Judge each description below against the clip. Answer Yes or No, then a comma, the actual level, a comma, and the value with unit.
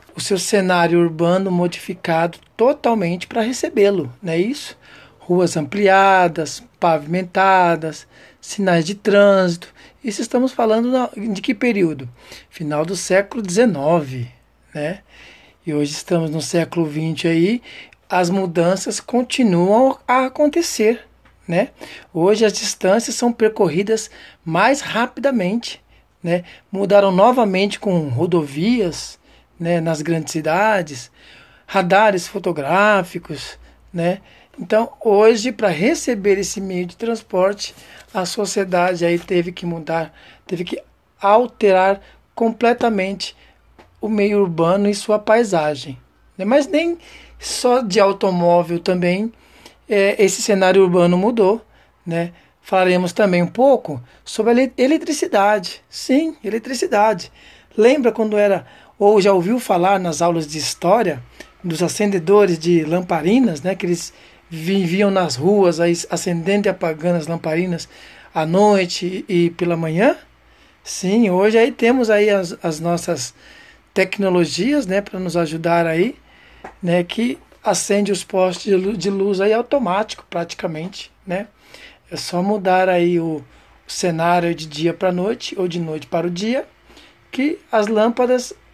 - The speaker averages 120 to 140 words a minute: Yes, average, 125 wpm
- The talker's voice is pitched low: No, high, 190 Hz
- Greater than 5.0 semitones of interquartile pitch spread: No, average, 4.1 semitones